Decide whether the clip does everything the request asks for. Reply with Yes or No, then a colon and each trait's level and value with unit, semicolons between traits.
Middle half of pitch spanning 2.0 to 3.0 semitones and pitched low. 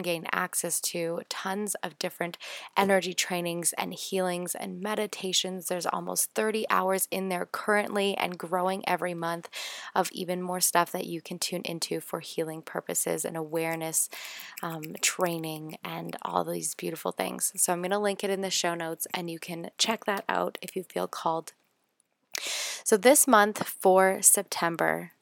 No: narrow, 2.5 semitones; medium, 180 Hz